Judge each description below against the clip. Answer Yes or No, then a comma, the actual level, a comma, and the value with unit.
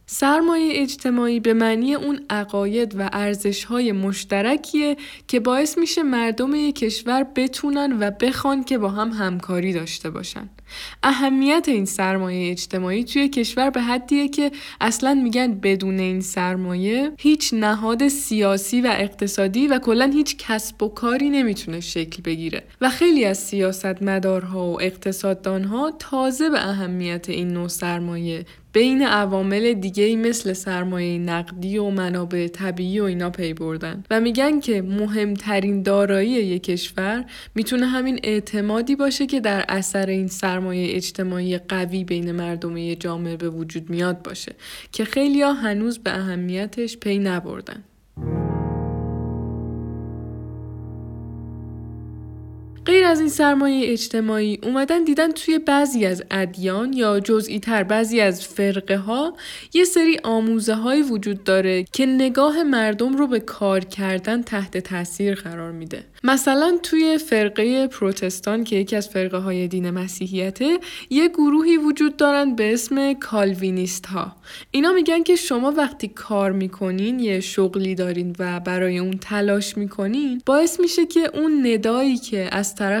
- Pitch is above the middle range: Yes, high, 210 Hz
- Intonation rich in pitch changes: Yes, wide, 6.0 semitones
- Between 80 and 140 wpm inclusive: Yes, average, 135 wpm